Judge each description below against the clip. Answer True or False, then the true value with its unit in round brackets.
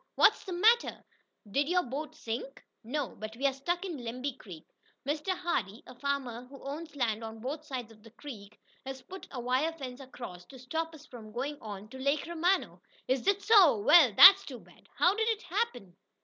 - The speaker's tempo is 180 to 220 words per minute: True (195 wpm)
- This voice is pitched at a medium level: False (270 Hz)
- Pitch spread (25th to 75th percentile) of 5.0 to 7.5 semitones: True (5.5 semitones)